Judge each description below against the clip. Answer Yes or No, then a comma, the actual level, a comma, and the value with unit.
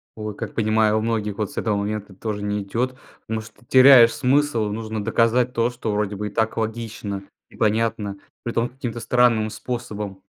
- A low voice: Yes, low, 110 Hz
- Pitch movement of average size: No, narrow, 2.1 semitones